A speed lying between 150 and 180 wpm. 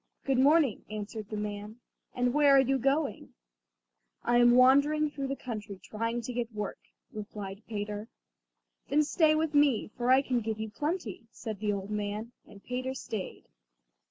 Yes: average, 170 wpm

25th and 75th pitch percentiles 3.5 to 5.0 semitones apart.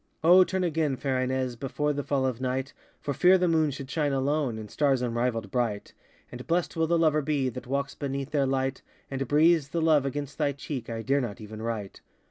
No: average, 3.1 semitones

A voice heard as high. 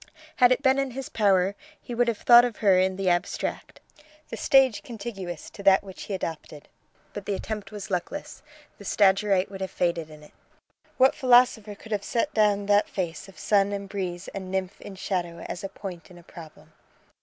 Yes: high, 200 Hz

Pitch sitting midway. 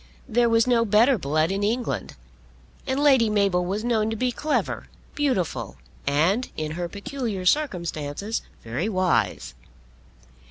No: high, 210 Hz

